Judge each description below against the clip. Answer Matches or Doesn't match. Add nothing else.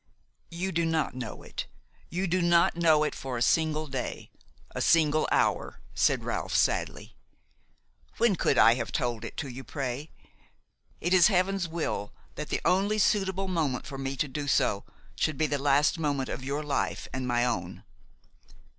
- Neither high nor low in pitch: Matches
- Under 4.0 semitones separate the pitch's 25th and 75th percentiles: Doesn't match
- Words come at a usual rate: Matches